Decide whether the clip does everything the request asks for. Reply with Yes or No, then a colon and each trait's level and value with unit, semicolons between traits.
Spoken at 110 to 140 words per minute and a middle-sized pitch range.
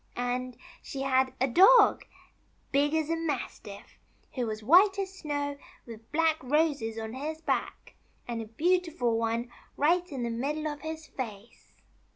No: average, 155 wpm; average, 5.0 semitones